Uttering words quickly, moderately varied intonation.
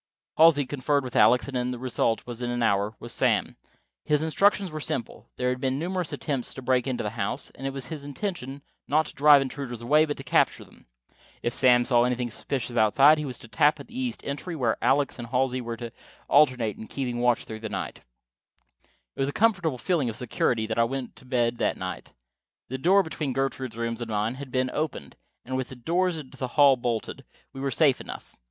Yes: fast, 215 wpm; average, 3.3 semitones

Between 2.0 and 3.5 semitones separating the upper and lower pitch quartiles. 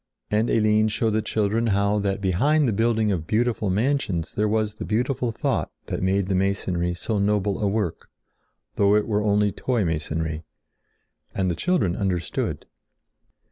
Yes: narrow, 2.6 semitones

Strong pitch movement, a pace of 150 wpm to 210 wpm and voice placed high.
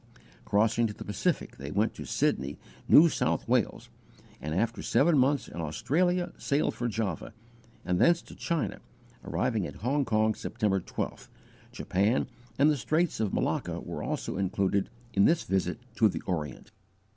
No: wide, 6.8 semitones; average, 160 wpm; low, 110 Hz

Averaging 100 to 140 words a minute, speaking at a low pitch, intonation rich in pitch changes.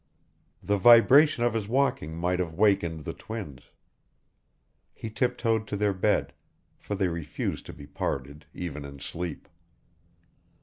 Yes: slow, 135 wpm; very low, 95 Hz; wide, 5.7 semitones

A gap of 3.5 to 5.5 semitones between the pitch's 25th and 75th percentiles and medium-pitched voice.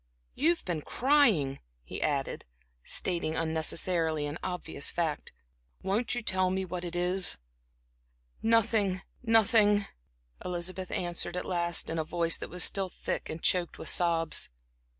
No: average, 2.9 semitones; medium, 180 Hz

